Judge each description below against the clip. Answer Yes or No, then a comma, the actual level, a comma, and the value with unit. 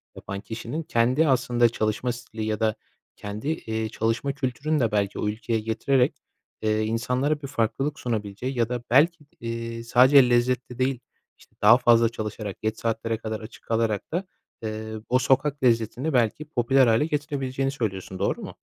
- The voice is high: No, low, 120 Hz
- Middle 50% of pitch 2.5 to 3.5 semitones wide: Yes, average, 3.2 semitones